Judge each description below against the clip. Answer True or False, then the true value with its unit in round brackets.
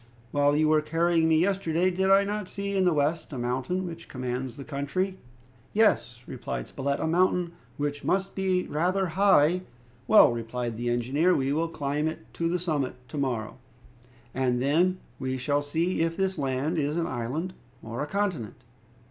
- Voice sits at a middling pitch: True (155 Hz)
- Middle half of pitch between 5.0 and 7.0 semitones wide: True (5.5 semitones)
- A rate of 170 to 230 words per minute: True (175 wpm)